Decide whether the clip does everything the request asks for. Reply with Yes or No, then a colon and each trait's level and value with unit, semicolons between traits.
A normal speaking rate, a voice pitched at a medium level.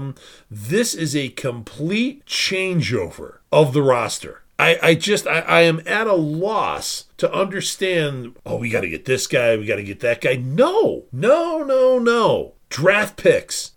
Yes: average, 155 wpm; medium, 165 Hz